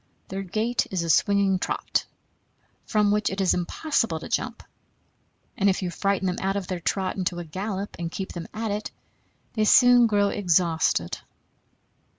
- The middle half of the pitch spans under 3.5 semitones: Yes, average, 2.8 semitones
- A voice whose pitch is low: No, high, 195 Hz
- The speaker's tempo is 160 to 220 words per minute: Yes, average, 165 wpm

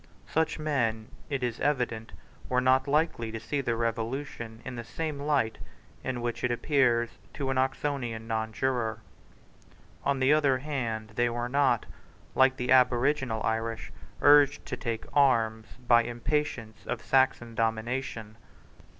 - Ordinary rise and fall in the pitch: Yes, average, 3.3 semitones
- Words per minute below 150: Yes, slow, 135 wpm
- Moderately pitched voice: No, low, 125 Hz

